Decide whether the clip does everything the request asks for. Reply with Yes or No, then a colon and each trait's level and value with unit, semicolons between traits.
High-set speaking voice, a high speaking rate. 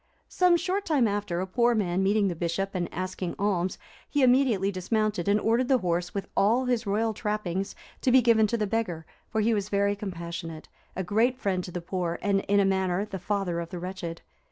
Yes: high, 200 Hz; fast, 210 wpm